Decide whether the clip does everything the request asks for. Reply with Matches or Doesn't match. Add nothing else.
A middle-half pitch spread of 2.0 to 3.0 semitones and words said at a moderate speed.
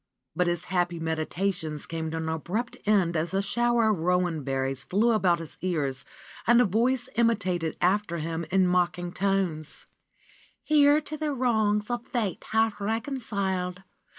Doesn't match